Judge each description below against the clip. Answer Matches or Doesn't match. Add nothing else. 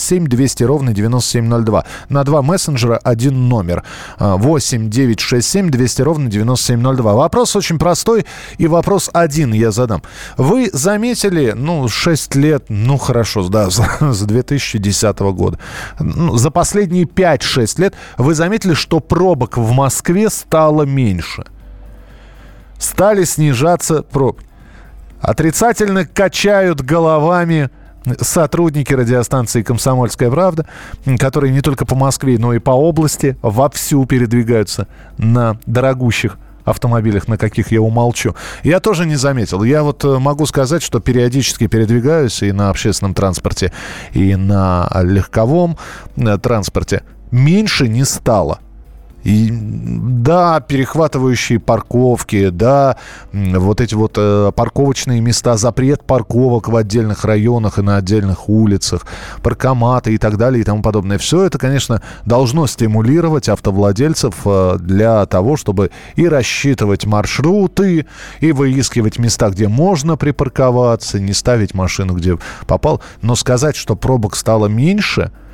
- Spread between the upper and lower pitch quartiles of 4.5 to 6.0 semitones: Matches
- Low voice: Matches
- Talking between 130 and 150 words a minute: Doesn't match